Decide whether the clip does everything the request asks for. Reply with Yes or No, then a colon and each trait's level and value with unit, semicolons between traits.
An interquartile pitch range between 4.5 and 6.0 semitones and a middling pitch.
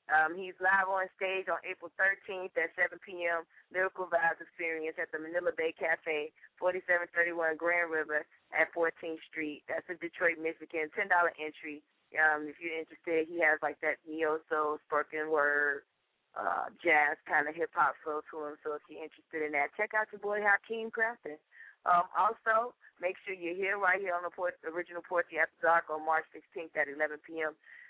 No: average, 2.9 semitones; medium, 165 Hz